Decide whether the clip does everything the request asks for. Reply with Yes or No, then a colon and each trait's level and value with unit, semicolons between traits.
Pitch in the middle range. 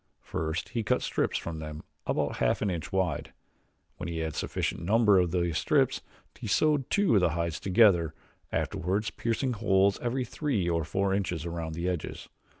No: very low, 95 Hz